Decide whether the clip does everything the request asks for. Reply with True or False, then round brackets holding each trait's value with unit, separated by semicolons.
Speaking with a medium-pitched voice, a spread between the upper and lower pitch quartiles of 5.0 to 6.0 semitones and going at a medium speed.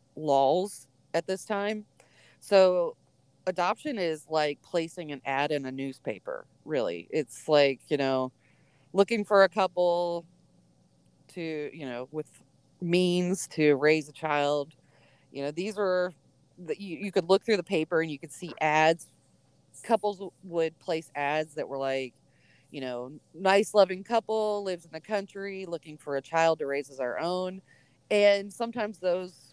True (165 Hz; 5.4 semitones; 155 wpm)